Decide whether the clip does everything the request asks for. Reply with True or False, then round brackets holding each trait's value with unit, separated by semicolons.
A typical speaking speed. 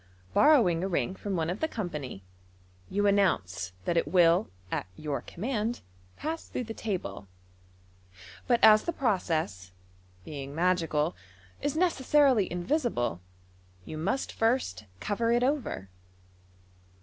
False (125 wpm)